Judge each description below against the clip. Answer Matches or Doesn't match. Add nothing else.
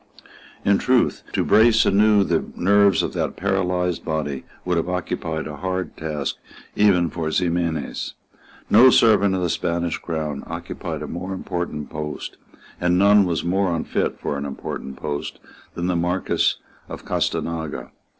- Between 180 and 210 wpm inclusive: Doesn't match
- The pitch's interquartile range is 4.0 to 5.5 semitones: Doesn't match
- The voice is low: Matches